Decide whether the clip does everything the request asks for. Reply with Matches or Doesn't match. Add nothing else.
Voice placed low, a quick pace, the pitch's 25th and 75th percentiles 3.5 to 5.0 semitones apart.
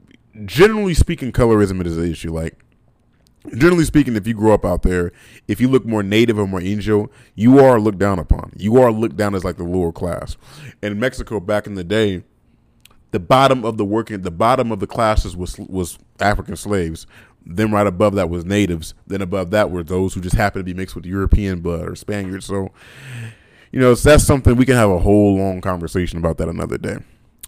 Matches